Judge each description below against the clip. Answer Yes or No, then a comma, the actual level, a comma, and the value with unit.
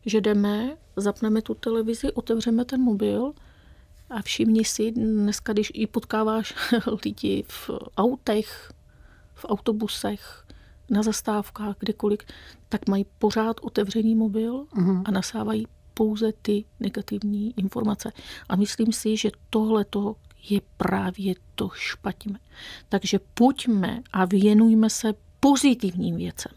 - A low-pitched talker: No, high, 220 Hz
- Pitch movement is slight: Yes, narrow, 1.5 semitones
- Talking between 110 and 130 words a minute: Yes, slow, 115 wpm